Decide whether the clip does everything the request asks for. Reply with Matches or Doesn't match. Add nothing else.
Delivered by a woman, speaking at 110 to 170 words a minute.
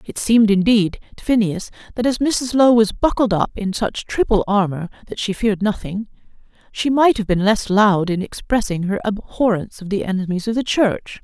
Doesn't match